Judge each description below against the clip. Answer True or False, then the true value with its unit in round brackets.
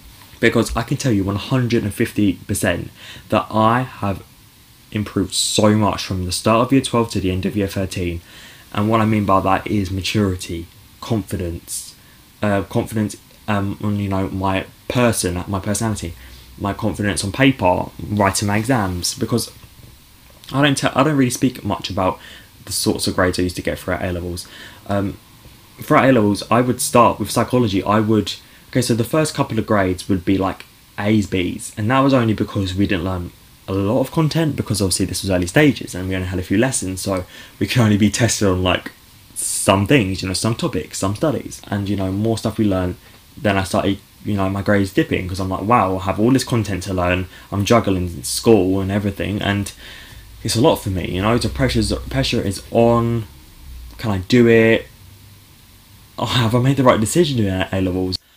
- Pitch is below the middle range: True (105 Hz)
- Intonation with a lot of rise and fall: False (3.3 semitones)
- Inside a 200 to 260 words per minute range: True (205 wpm)